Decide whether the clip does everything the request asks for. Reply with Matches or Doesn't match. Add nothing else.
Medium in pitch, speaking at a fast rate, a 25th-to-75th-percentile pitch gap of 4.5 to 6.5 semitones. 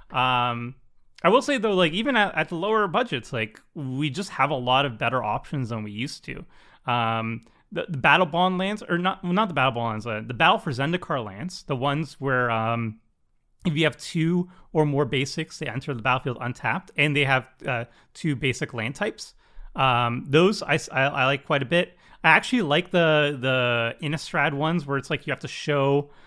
Matches